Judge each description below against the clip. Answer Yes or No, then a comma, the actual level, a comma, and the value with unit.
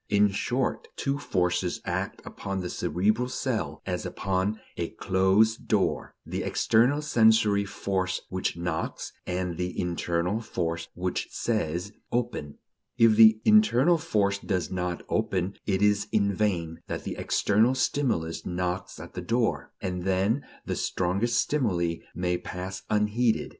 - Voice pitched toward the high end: No, low, 100 Hz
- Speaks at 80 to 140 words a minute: Yes, slow, 135 wpm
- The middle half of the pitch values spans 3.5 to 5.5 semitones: Yes, average, 3.9 semitones